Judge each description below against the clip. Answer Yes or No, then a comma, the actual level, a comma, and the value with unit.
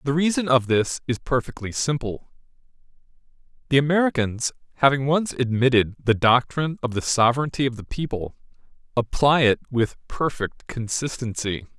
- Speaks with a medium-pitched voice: No, low, 125 Hz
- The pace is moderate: No, slow, 125 wpm